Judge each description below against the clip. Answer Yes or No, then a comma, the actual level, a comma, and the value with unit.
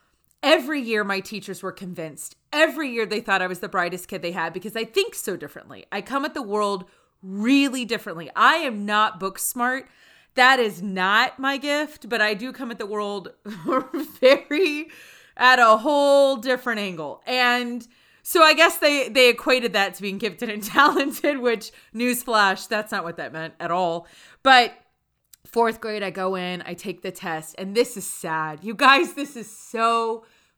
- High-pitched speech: Yes, high, 225 Hz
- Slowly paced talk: No, average, 185 wpm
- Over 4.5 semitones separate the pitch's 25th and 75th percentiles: Yes, wide, 5.4 semitones